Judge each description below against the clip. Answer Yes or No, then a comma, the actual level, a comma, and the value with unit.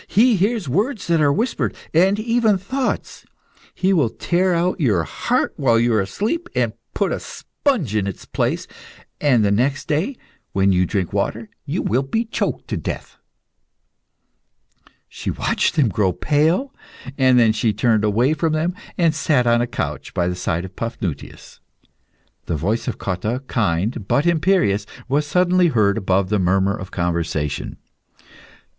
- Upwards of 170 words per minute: No, average, 160 wpm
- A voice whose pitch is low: Yes, low, 125 Hz